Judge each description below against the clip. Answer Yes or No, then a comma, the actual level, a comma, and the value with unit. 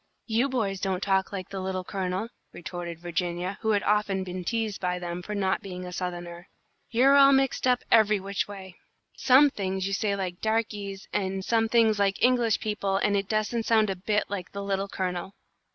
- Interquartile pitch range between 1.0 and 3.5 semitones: Yes, average, 2.7 semitones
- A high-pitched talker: Yes, high, 195 Hz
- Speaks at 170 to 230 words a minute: Yes, average, 195 wpm